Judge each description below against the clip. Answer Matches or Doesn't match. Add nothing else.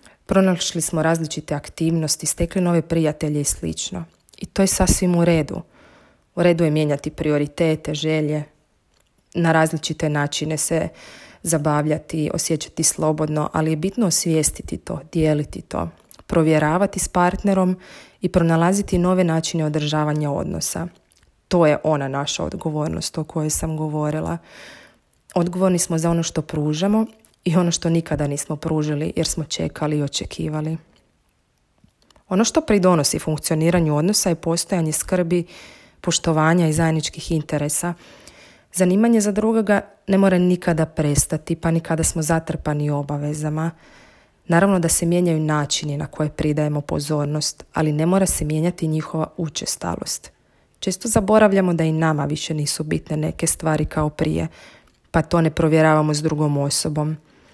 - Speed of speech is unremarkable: Matches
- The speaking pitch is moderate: Matches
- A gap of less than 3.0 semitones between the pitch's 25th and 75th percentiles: Matches